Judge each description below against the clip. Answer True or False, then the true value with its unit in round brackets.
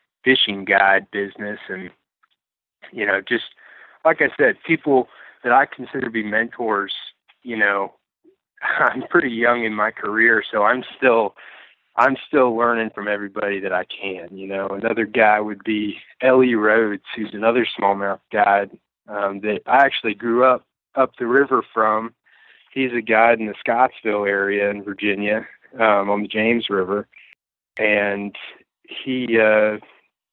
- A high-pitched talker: False (105 Hz)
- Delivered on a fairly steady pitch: True (2.3 semitones)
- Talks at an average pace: True (150 wpm)